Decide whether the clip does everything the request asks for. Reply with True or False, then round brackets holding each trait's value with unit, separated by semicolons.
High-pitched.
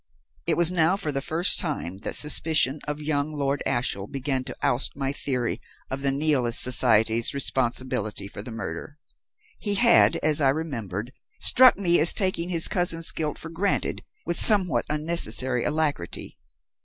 False (145 Hz)